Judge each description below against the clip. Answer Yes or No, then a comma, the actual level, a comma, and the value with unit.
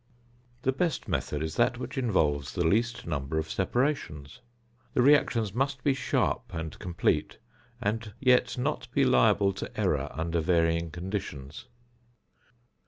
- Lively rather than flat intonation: Yes, wide, 7.6 semitones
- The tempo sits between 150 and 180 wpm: No, slow, 135 wpm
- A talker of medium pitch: No, low, 100 Hz